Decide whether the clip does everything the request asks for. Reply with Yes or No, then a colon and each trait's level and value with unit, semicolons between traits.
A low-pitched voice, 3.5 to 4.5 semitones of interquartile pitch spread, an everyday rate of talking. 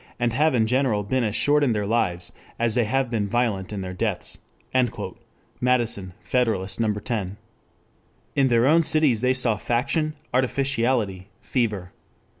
Yes: low, 120 Hz; average, 4.0 semitones; average, 150 wpm